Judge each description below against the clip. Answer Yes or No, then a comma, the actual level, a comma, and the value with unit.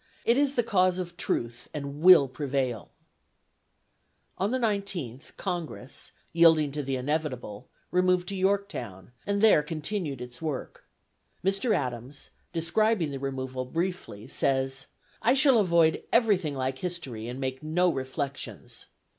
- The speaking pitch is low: No, medium, 155 Hz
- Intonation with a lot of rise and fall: Yes, wide, 6.0 semitones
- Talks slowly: Yes, slow, 130 wpm